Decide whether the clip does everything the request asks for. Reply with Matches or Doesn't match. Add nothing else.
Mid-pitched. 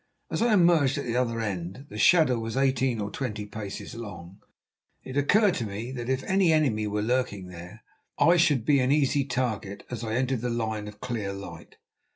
Doesn't match